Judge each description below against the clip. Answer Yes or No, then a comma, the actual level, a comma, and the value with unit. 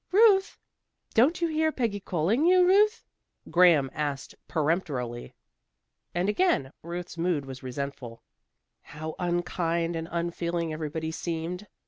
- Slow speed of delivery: Yes, slow, 115 wpm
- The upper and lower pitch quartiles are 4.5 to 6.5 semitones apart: Yes, average, 5.3 semitones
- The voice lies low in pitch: No, medium, 170 Hz